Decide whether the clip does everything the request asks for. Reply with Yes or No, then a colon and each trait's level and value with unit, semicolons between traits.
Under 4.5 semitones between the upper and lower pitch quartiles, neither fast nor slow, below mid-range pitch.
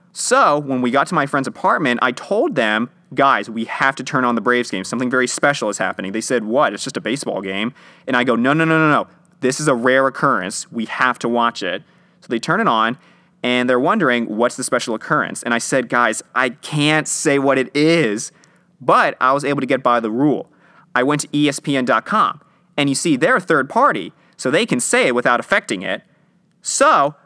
No: average, 3.5 semitones; fast, 225 wpm; low, 130 Hz